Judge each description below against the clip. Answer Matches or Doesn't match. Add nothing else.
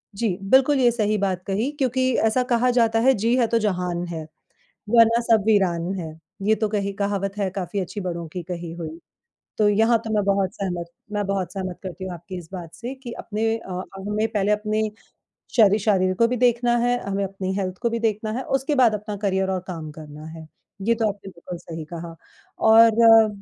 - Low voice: Doesn't match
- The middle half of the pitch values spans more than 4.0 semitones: Doesn't match